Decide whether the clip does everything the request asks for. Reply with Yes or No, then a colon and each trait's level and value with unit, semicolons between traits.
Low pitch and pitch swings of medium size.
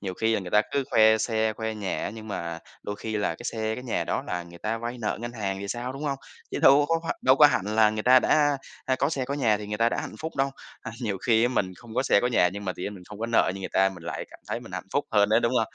Yes: low, 110 Hz; average, 3.5 semitones